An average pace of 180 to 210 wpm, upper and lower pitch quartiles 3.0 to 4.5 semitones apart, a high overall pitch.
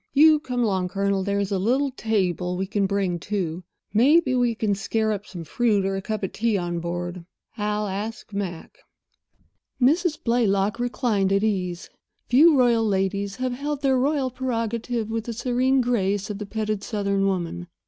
No: average, 170 wpm; average, 4.0 semitones; high, 210 Hz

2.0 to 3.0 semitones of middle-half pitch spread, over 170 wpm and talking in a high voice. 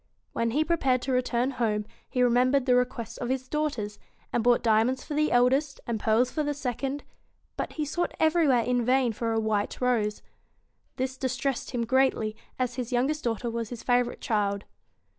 Yes: narrow, 2.5 semitones; average, 185 wpm; very high, 250 Hz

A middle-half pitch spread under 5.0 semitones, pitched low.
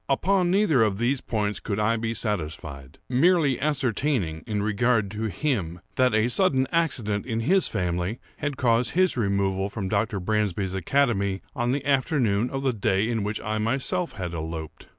No: average, 5.3 semitones; low, 110 Hz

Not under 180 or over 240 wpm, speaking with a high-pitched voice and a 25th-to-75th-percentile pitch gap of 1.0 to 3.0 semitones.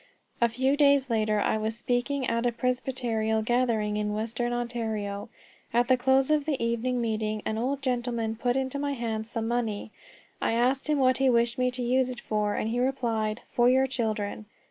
Yes: average, 190 wpm; high, 240 Hz; average, 2.7 semitones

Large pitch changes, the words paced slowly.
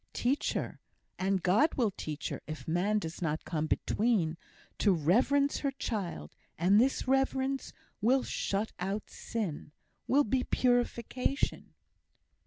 Yes: wide, 6.9 semitones; slow, 130 wpm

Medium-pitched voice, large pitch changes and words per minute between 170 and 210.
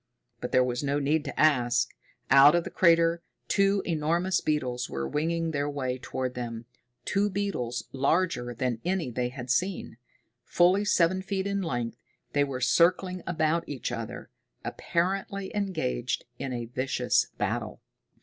No: medium, 150 Hz; wide, 6.3 semitones; average, 150 wpm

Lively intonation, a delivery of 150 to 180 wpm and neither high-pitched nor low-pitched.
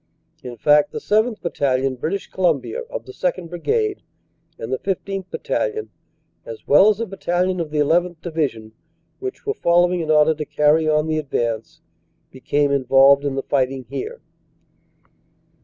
Yes: wide, 5.8 semitones; average, 160 wpm; medium, 160 Hz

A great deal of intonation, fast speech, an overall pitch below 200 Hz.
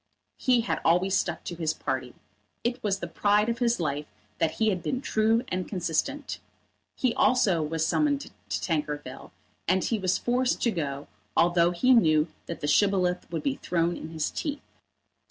No: wide, 6.4 semitones; average, 175 wpm; medium, 185 Hz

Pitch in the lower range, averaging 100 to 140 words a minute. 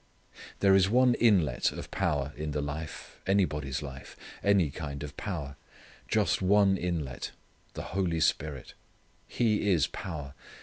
Yes: very low, 80 Hz; slow, 135 wpm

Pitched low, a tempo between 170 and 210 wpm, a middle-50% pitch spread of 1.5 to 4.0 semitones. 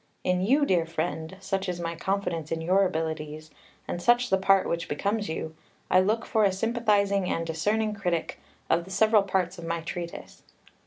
No: medium, 185 Hz; average, 180 wpm; average, 3.3 semitones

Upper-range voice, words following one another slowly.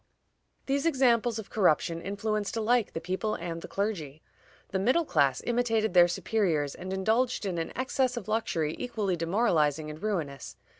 No: high, 200 Hz; average, 155 wpm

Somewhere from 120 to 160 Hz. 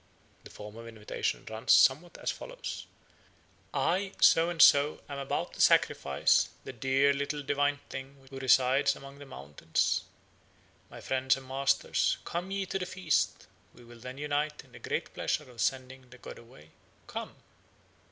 Yes: low, 135 Hz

